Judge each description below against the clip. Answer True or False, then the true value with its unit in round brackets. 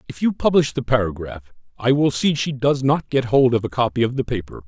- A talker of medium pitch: False (125 Hz)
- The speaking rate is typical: False (245 wpm)